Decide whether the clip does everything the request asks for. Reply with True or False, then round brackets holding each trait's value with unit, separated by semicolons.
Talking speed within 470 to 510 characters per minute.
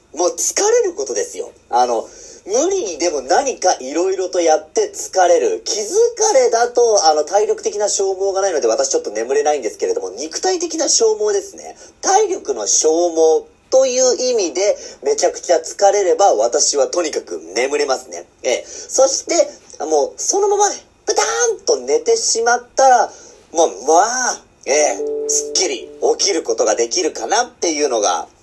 False (330 characters per minute)